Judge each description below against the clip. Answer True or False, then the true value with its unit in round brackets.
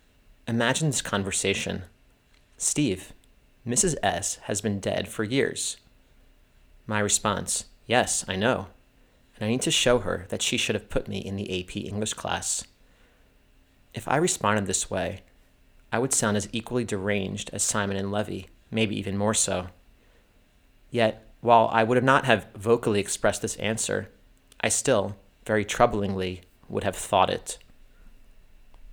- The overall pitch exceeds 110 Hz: False (105 Hz)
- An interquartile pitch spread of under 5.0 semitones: True (2.8 semitones)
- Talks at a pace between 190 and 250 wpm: False (145 wpm)